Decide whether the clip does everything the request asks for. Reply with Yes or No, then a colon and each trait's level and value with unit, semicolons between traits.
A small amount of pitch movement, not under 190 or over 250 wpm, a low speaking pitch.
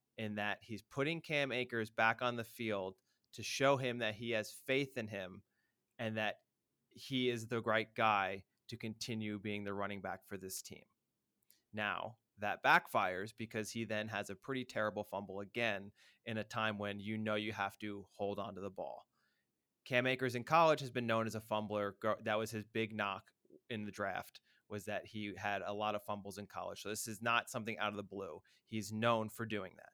Yes: narrow, 2.3 semitones; fast, 205 wpm; low, 110 Hz